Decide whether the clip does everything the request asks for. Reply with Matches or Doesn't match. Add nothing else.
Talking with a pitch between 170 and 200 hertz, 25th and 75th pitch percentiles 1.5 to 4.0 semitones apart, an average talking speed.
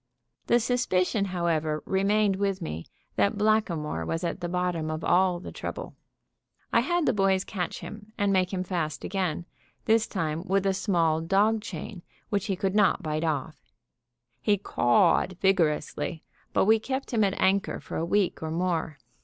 Matches